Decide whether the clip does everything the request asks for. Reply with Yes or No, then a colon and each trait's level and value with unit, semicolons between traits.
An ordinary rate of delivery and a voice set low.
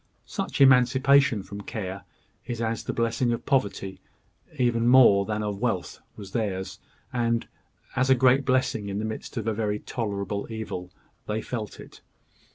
Yes: average, 155 wpm; low, 115 Hz